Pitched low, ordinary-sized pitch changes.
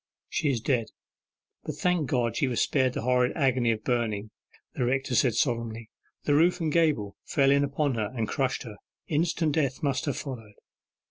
Yes: low, 130 Hz; average, 3.8 semitones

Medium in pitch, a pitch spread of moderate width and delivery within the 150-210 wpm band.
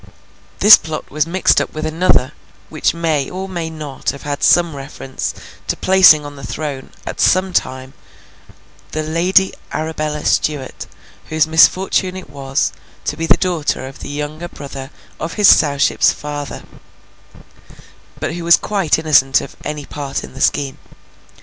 Yes: medium, 155 Hz; average, 3.1 semitones; average, 155 wpm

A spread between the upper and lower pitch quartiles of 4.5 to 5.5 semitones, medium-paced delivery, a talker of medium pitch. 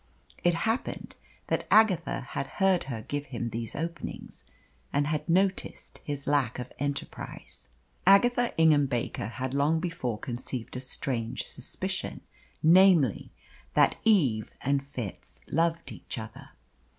No: average, 5.2 semitones; slow, 125 wpm; medium, 145 Hz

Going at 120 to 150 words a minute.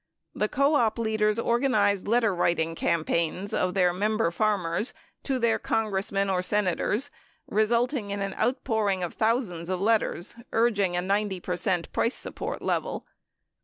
Yes: average, 140 wpm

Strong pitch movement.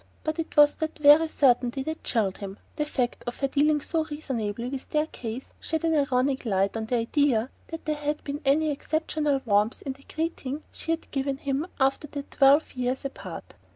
No: average, 3.4 semitones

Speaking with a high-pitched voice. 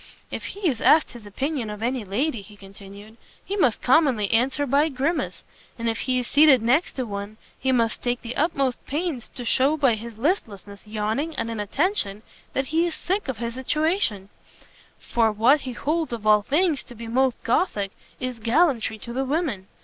Yes: high, 245 Hz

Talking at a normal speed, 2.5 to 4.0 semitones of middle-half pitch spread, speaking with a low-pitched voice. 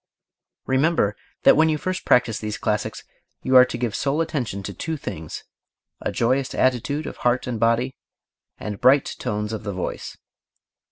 No: average, 160 wpm; average, 4.8 semitones; low, 125 Hz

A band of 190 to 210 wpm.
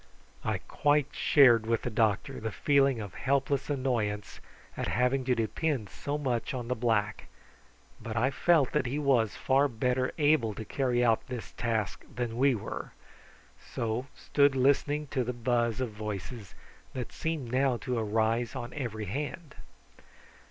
No: average, 155 wpm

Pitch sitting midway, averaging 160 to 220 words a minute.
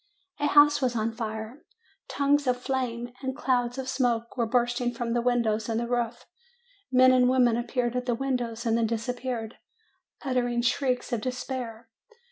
No: high, 245 Hz; average, 165 wpm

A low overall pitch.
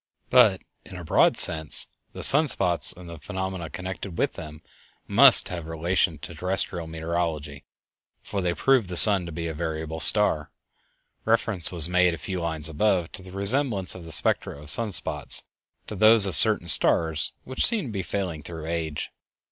Yes: very low, 90 Hz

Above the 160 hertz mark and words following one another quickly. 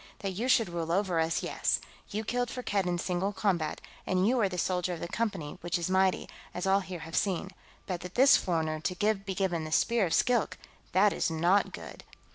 Yes: medium, 185 Hz; fast, 210 wpm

